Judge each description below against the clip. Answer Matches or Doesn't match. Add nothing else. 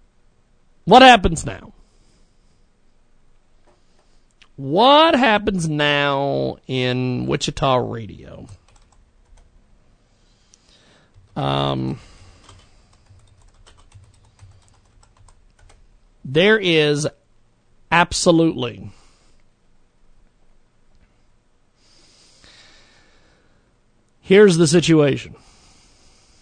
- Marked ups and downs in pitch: Matches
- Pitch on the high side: Doesn't match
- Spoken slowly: Matches